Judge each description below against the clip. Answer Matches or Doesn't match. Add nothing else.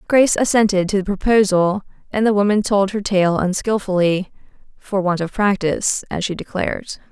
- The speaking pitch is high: Matches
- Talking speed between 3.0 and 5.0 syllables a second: Doesn't match